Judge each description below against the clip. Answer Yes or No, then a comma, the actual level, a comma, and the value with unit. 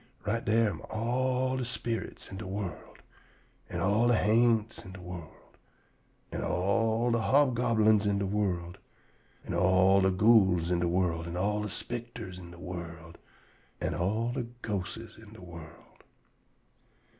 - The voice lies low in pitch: Yes, low, 105 Hz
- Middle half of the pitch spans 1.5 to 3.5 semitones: No, average, 4.2 semitones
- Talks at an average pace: Yes, average, 155 wpm